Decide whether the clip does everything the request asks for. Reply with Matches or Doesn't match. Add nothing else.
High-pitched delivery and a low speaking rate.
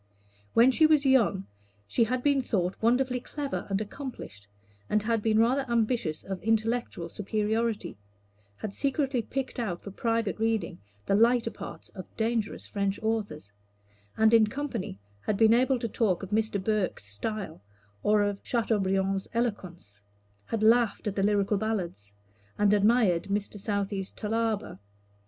Doesn't match